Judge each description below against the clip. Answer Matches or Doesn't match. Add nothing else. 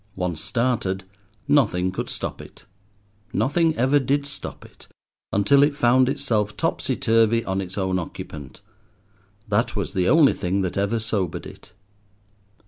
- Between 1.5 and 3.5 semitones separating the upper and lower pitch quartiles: Doesn't match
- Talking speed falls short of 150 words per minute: Matches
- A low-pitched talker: Matches